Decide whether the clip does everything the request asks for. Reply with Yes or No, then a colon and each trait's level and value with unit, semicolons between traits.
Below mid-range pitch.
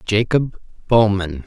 Yes: low, 105 Hz